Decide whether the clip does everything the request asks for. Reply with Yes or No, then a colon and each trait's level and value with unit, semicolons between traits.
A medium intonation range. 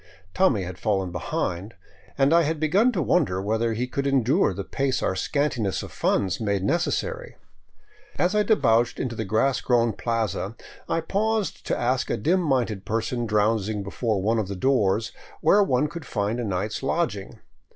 No: wide, 6.3 semitones